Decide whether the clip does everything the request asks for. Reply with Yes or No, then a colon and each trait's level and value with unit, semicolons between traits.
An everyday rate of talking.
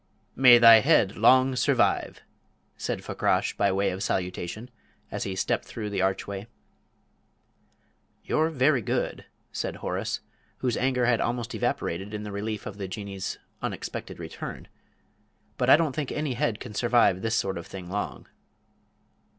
Yes: average, 150 wpm